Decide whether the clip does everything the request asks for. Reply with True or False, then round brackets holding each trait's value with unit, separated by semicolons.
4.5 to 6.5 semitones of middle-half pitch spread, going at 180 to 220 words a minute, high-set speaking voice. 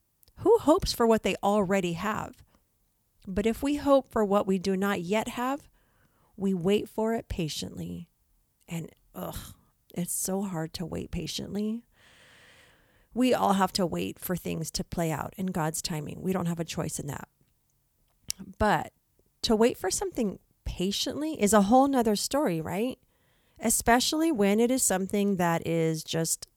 False (5.1 semitones; 160 wpm; 200 Hz)